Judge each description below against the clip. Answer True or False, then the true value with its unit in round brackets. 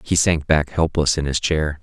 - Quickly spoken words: True (230 wpm)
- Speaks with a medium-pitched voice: False (75 Hz)